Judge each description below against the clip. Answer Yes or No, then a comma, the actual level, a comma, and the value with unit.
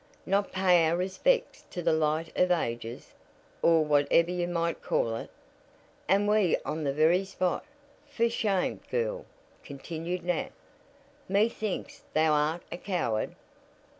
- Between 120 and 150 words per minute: Yes, slow, 135 wpm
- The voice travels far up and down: No, average, 3.7 semitones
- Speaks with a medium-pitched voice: Yes, medium, 175 Hz